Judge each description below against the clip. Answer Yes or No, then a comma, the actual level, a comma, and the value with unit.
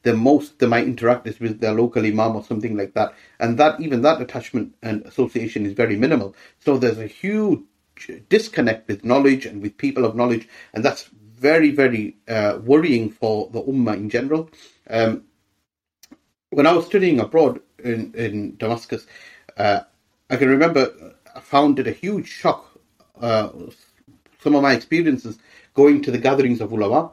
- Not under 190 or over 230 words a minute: No, average, 170 wpm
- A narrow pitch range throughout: No, average, 4.0 semitones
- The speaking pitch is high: No, low, 120 Hz